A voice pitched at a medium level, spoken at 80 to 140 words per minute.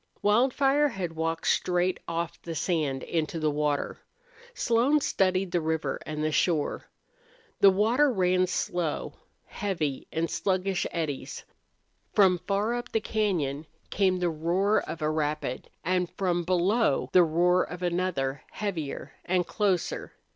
Yes: medium, 180 Hz; slow, 135 wpm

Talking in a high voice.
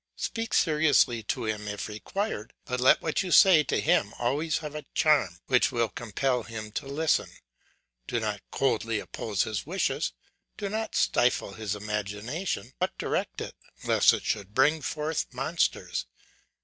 No: low, 125 Hz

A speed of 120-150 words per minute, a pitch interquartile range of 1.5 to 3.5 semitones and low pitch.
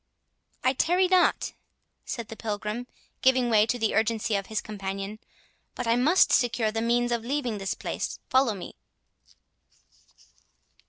No: average, 140 wpm; average, 2.7 semitones; high, 230 Hz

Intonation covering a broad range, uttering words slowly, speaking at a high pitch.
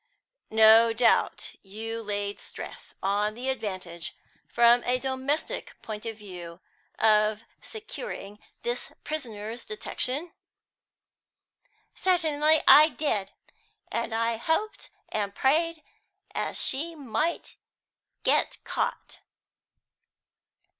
Yes: wide, 6.3 semitones; slow, 90 wpm; high, 230 Hz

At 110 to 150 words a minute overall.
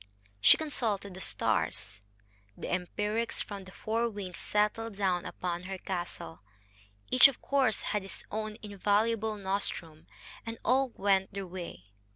Yes: average, 140 wpm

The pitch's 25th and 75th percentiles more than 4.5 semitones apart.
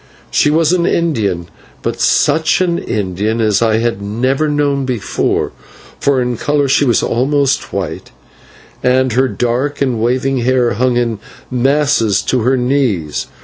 No: average, 3.8 semitones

